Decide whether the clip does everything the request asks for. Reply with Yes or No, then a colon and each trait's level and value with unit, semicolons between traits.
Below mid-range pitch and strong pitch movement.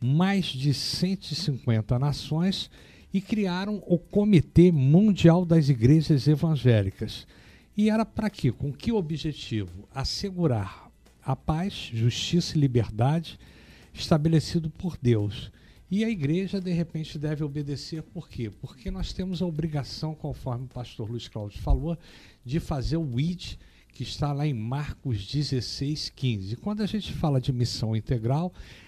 No: medium, 150 Hz; wide, 5.8 semitones